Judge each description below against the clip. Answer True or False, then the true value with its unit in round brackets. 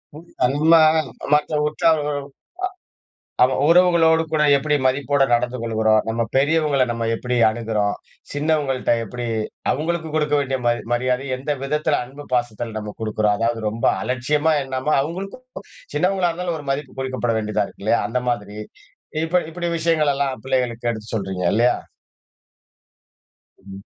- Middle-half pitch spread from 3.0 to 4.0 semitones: False (4.6 semitones)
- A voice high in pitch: False (135 Hz)